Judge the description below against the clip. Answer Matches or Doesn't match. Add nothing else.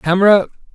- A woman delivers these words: Doesn't match